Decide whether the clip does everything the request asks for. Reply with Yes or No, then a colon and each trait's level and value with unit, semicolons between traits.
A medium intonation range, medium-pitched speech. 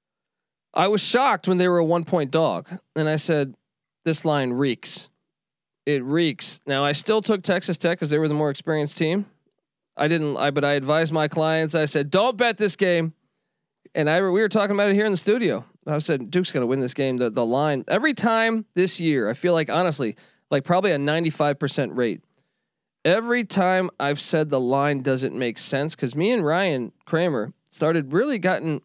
Yes: average, 4.3 semitones; medium, 160 Hz